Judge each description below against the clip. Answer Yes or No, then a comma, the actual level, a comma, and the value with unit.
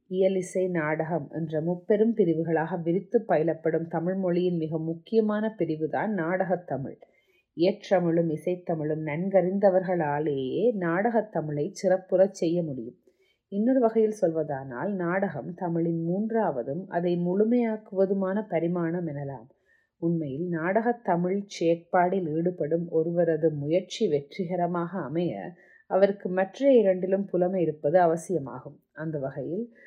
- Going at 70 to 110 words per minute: Yes, average, 100 wpm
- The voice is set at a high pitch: No, medium, 180 Hz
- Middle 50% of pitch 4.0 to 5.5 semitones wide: No, average, 2.9 semitones